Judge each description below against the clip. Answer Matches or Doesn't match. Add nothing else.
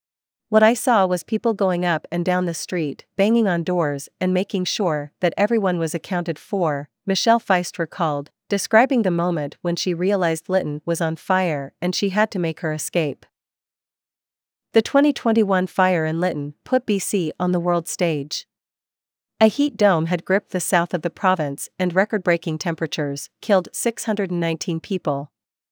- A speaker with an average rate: Matches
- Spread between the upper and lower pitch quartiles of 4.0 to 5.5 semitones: Doesn't match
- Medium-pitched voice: Matches